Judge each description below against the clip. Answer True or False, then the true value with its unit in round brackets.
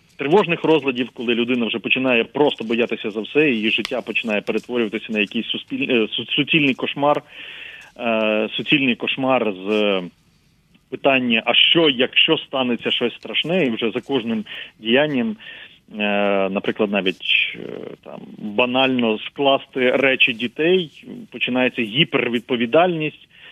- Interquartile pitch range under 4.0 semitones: False (4.4 semitones)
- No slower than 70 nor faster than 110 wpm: True (105 wpm)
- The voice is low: True (125 Hz)